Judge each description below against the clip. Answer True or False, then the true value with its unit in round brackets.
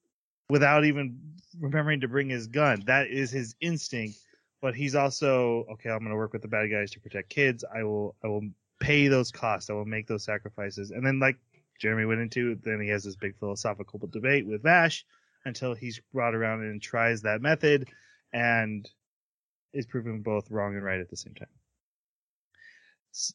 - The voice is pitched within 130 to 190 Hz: False (115 Hz)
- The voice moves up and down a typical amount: True (4.5 semitones)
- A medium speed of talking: True (185 wpm)